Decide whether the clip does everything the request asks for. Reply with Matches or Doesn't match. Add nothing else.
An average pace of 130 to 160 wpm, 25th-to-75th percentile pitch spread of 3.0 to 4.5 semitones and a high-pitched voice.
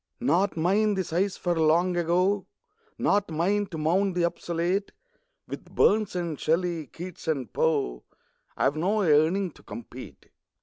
Doesn't match